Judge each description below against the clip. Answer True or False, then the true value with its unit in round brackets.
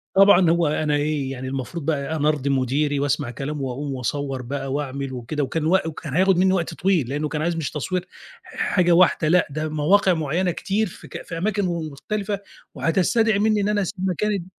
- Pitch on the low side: False (155 Hz)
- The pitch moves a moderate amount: True (4.7 semitones)